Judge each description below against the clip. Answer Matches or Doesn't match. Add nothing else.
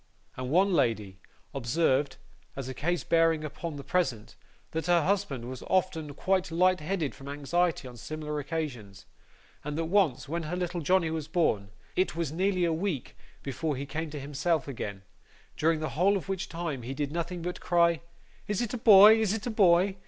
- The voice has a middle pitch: Matches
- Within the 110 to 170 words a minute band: Doesn't match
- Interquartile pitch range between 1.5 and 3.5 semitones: Doesn't match